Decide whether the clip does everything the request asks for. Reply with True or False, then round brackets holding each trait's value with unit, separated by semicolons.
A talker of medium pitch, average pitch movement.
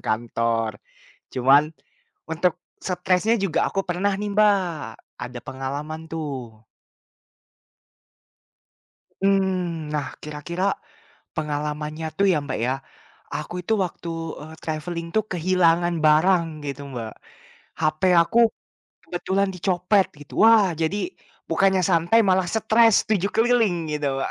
True (170 Hz; 4.3 semitones)